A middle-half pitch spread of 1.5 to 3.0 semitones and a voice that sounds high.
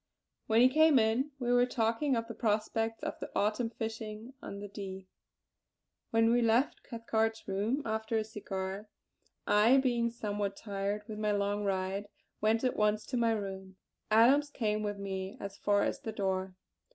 Yes: narrow, 2.4 semitones; high, 220 Hz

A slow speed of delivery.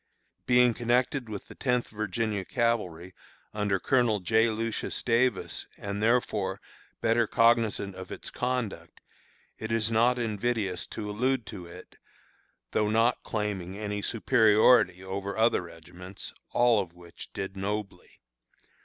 Yes: slow, 125 wpm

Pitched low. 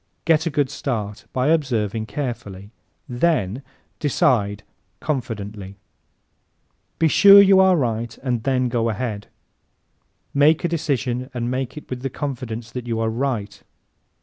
Yes: low, 125 Hz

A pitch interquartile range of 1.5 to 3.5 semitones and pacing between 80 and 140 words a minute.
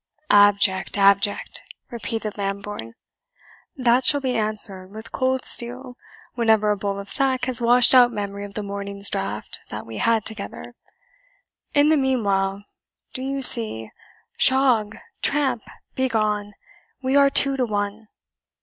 No: average, 4.2 semitones; slow, 135 wpm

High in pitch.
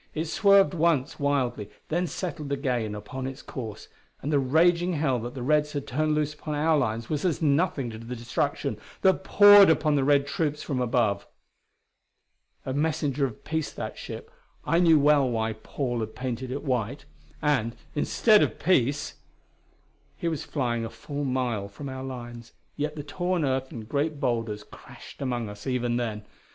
No: medium, 140 Hz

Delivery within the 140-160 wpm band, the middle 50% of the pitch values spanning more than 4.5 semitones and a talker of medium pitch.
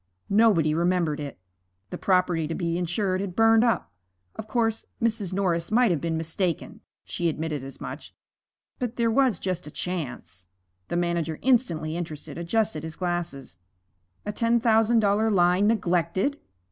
Yes: average, 150 wpm; average, 5.1 semitones; medium, 180 Hz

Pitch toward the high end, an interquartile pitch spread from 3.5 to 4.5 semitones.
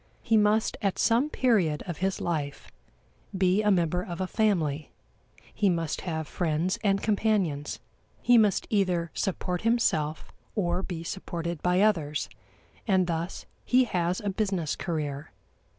No: medium, 180 Hz; average, 4.0 semitones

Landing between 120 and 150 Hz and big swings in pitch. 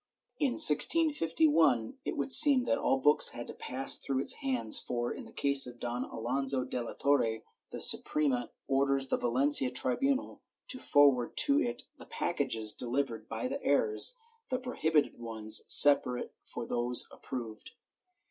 No: low, 135 Hz; average, 5.0 semitones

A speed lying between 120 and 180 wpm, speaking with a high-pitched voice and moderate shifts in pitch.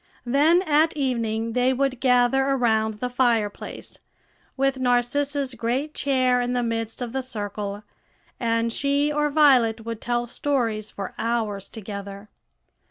Yes: slow, 135 wpm; high, 245 Hz; average, 3.3 semitones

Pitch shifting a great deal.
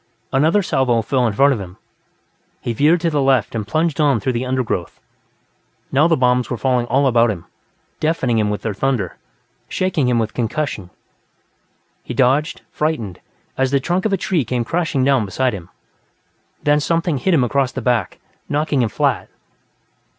No: average, 4.4 semitones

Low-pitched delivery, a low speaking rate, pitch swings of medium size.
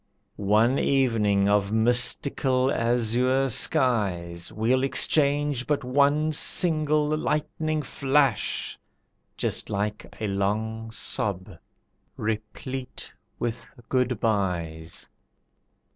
Yes: low, 120 Hz; slow, 85 wpm; average, 4.8 semitones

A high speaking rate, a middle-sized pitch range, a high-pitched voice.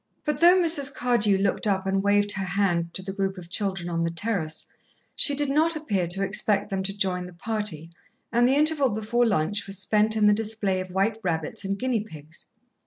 Yes: fast, 210 wpm; average, 3.3 semitones; high, 200 Hz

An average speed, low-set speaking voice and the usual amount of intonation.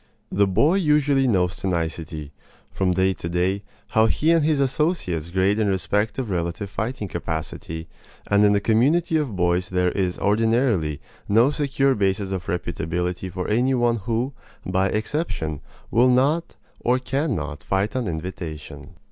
No: average, 155 wpm; low, 100 Hz; wide, 6.3 semitones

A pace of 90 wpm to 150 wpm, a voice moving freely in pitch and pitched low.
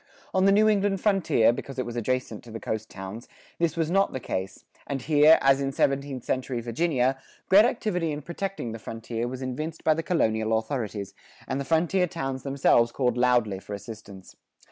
No: average, 190 wpm; wide, 6.1 semitones; low, 130 Hz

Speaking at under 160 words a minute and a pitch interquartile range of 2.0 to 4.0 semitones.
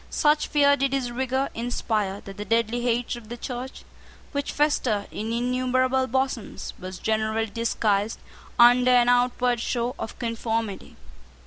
Yes: average, 140 wpm; narrow, 2.5 semitones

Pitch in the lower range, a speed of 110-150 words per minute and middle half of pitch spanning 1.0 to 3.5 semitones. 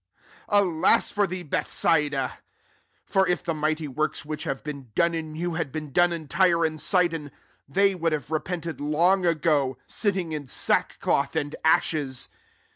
No: medium, 160 Hz; average, 145 wpm; average, 2.8 semitones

